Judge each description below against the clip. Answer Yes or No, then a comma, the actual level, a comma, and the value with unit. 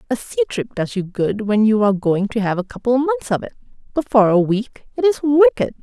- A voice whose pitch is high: Yes, high, 240 Hz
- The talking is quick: Yes, fast, 255 wpm